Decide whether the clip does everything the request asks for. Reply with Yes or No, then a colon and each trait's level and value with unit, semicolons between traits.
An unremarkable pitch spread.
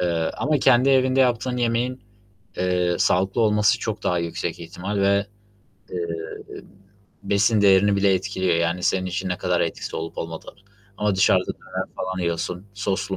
Yes: average, 3.2 semitones